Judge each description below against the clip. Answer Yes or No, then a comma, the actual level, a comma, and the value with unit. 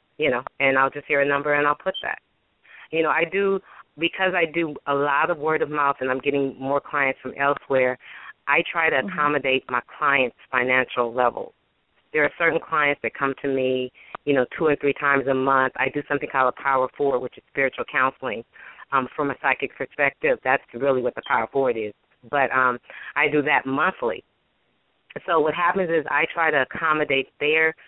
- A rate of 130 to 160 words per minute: No, average, 200 wpm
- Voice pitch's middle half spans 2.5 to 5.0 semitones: Yes, average, 2.8 semitones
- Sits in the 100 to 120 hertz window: No, medium, 140 Hz